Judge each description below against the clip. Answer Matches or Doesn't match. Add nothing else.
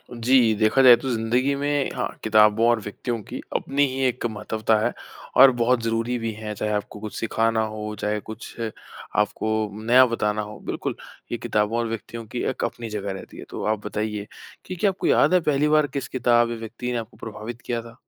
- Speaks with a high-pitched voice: Doesn't match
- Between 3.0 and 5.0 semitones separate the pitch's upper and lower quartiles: Doesn't match